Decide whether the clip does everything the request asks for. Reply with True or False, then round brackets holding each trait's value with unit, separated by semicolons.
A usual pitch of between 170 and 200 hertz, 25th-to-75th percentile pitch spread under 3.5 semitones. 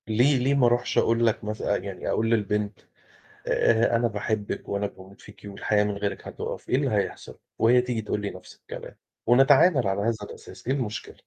False (110 Hz; 3.0 semitones)